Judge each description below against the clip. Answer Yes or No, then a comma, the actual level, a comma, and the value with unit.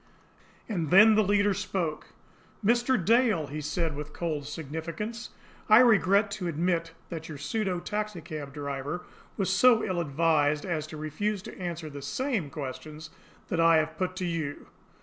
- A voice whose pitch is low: No, medium, 170 Hz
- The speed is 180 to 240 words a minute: No, average, 155 wpm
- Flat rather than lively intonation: No, average, 4.9 semitones